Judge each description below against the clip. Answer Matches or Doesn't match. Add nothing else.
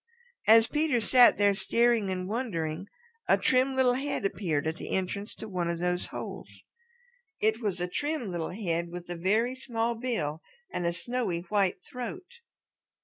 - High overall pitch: Matches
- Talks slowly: Doesn't match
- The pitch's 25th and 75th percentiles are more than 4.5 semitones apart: Matches